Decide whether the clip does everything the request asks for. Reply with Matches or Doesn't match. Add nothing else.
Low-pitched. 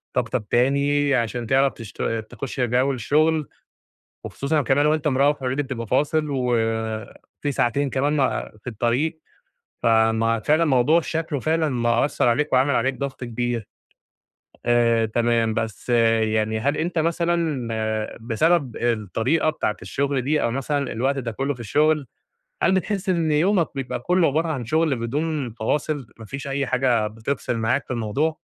Matches